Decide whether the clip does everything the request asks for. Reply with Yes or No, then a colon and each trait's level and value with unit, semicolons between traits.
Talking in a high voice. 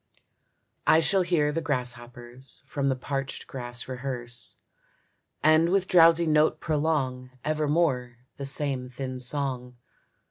No: low, 135 Hz